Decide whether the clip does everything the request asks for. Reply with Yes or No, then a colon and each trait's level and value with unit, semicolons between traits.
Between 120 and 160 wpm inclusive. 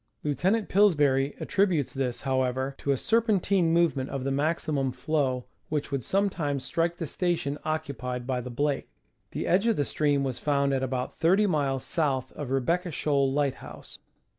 No: average, 170 wpm